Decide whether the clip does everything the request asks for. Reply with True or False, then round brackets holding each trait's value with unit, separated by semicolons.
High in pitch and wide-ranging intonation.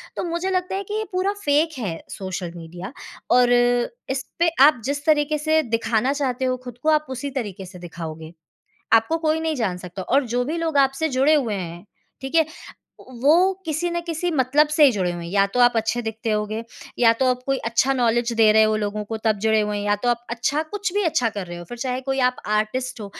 True (245 Hz; 6.2 semitones)